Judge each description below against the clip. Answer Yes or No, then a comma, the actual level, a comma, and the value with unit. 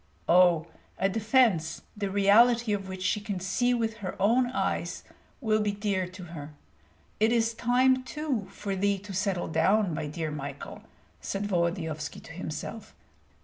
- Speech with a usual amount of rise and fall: Yes, average, 4.1 semitones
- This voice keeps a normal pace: Yes, average, 155 wpm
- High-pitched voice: Yes, high, 200 Hz